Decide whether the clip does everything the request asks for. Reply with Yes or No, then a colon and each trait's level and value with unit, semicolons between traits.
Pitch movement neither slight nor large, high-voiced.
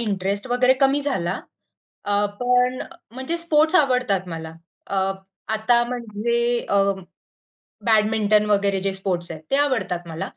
Yes: average, 4.3 semitones; high, 220 Hz